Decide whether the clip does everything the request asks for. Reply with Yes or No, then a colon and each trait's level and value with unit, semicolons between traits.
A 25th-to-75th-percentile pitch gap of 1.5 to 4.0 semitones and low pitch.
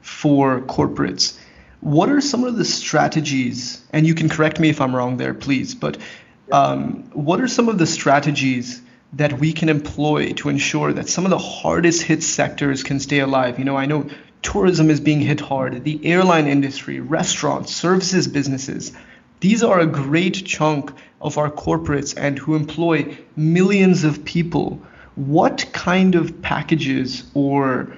No: average, 3.3 semitones; medium, 150 Hz